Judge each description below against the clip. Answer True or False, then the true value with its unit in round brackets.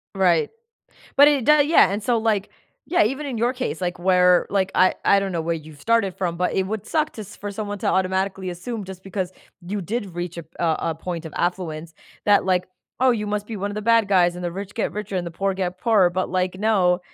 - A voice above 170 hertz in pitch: True (190 Hz)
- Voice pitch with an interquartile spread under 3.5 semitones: True (3.0 semitones)